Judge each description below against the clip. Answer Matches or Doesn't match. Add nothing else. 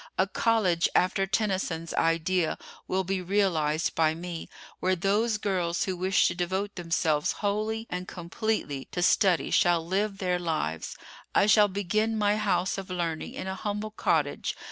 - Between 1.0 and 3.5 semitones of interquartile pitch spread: Matches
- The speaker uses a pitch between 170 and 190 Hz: Matches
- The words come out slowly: Doesn't match